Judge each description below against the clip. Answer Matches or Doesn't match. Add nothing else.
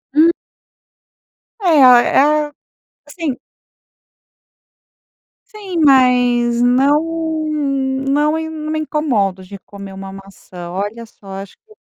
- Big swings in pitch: Matches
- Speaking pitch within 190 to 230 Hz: Doesn't match